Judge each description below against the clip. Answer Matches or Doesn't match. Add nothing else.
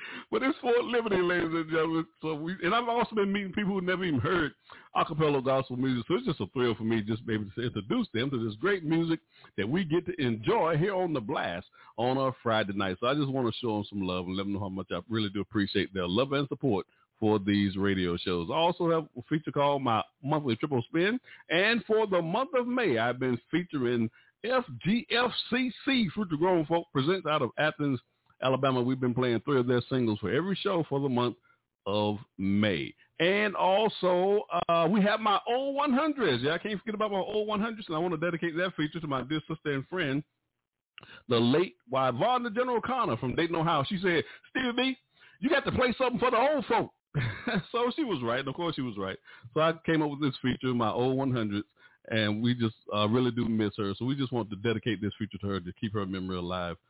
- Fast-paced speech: Matches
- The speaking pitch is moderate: Matches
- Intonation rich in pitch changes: Matches